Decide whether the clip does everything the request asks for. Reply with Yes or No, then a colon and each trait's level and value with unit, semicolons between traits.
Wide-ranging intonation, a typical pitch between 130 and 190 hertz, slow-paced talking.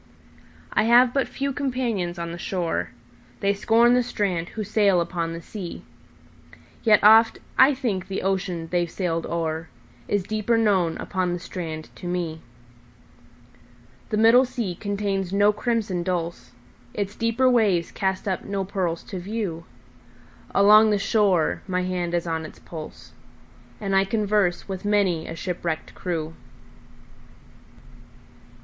No: average, 4.1 semitones; medium, 185 Hz; slow, 125 wpm